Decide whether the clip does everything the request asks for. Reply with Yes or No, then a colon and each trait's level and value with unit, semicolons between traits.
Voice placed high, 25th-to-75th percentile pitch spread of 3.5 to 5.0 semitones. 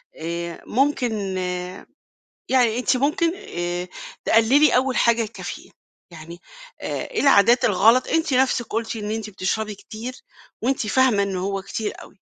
Yes: high, 225 Hz; average, 4.7 semitones